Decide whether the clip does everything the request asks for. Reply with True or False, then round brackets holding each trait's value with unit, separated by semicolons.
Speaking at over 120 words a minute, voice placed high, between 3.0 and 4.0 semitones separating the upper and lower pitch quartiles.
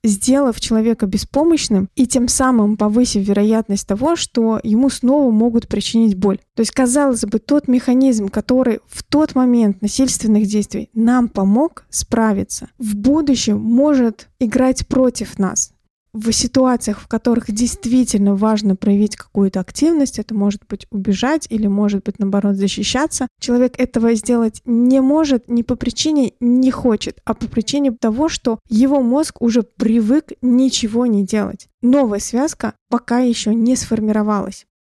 True (140 wpm; 235 Hz; 3.3 semitones)